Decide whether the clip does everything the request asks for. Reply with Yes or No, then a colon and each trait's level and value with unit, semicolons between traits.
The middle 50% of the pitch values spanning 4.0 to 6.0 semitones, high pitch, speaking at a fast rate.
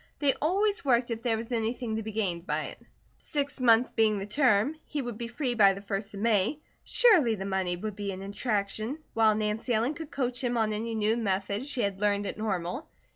No: average, 3.6 semitones; high, 220 Hz; fast, 220 wpm